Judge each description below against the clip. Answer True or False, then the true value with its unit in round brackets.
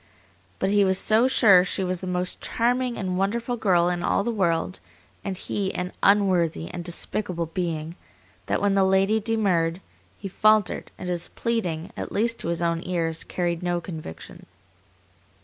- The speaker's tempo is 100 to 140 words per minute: False (170 wpm)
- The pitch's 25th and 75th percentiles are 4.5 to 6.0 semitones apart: False (3.2 semitones)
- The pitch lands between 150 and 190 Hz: True (185 Hz)